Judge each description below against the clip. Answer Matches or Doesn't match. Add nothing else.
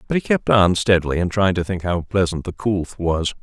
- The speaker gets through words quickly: Matches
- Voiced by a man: Matches